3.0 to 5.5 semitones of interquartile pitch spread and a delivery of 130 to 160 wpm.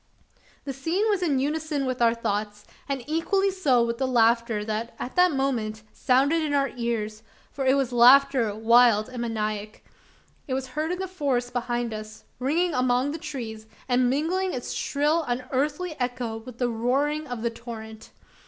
No: average, 3.9 semitones; average, 170 wpm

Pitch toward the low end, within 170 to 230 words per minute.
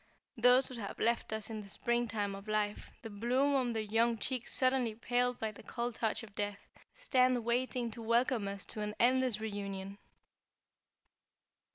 No: high, 230 Hz; average, 175 wpm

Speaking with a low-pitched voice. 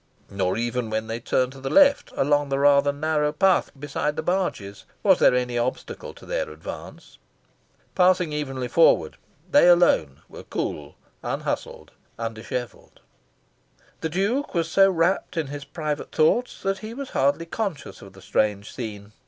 No: medium, 145 Hz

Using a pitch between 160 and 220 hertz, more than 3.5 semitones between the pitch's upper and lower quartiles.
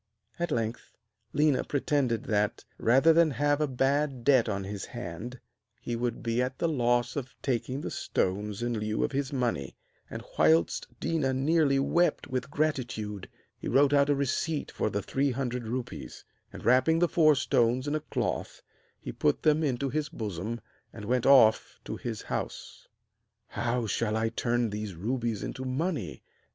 No: low, 125 Hz; average, 4.1 semitones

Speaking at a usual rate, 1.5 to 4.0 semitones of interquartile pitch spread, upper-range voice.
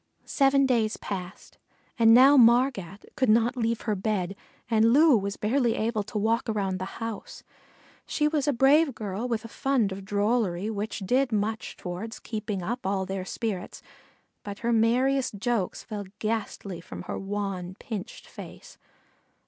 Yes: average, 155 wpm; average, 3.5 semitones; high, 220 Hz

